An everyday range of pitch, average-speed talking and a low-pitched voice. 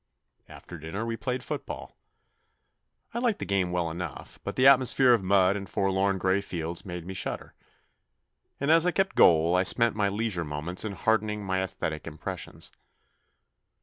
Yes: average, 4.4 semitones; average, 165 wpm; very low, 95 Hz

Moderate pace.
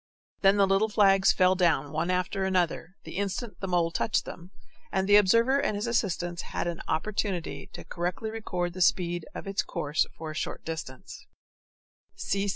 Yes: average, 170 wpm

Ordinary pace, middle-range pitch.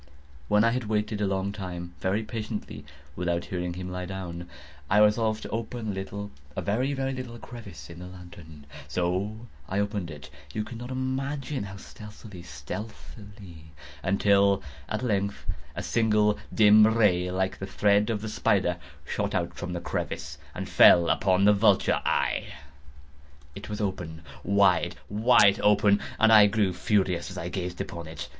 No: average, 155 wpm; low, 100 Hz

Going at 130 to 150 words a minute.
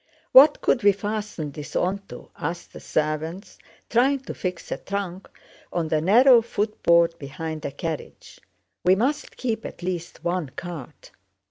Yes: average, 145 wpm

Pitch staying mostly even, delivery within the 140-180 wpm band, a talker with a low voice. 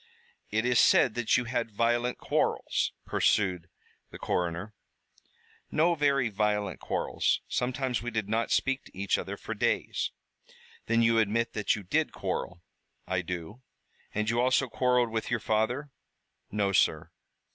No: average, 3.5 semitones; average, 145 wpm; low, 115 Hz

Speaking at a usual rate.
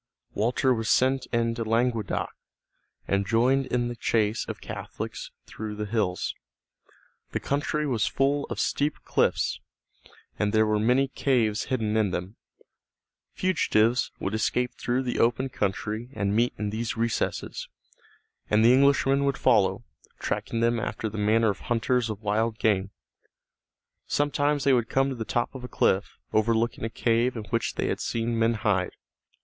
Yes: average, 155 wpm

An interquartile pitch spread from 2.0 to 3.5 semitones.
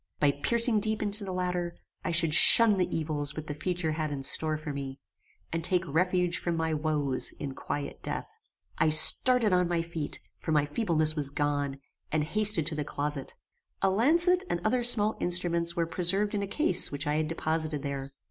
No: average, 4.2 semitones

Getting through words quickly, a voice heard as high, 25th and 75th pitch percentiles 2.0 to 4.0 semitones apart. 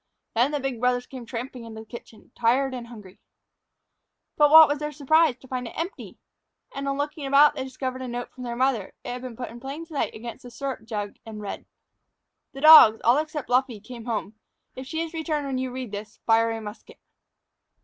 Yes: fast, 210 wpm; very high, 255 Hz; average, 3.3 semitones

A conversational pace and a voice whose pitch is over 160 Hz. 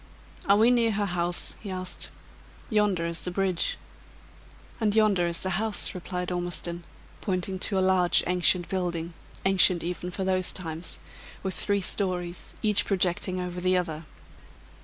Yes: average, 150 wpm; medium, 185 Hz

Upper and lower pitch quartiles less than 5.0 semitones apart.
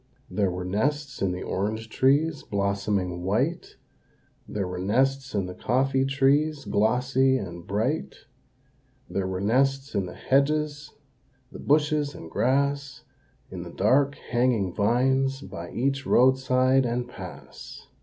No: wide, 5.4 semitones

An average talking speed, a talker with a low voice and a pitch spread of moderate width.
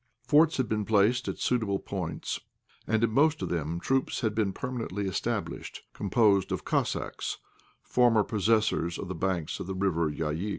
Yes: average, 165 wpm; low, 105 Hz; average, 3.9 semitones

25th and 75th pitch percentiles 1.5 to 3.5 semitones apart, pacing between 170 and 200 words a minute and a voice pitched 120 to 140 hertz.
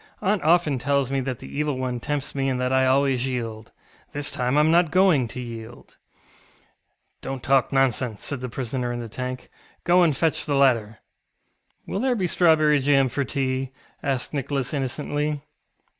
Yes: average, 2.8 semitones; average, 175 wpm; low, 135 Hz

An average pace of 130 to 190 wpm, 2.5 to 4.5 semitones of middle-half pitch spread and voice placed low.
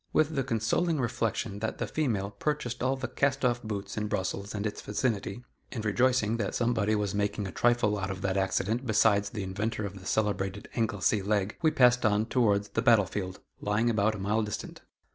No: average, 200 wpm; average, 3.1 semitones; low, 105 Hz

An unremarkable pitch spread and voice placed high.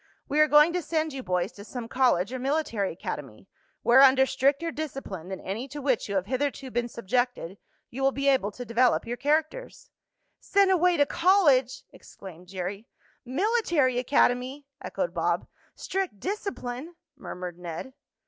No: wide, 6.0 semitones; very high, 260 Hz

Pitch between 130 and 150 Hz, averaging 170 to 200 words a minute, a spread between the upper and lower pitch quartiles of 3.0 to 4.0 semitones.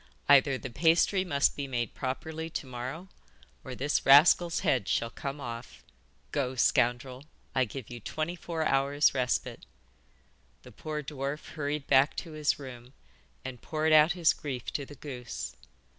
No: medium, 140 Hz; average, 155 wpm; average, 3.3 semitones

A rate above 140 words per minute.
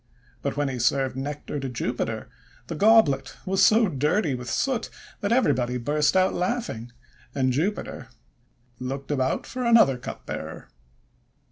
No: slow, 135 wpm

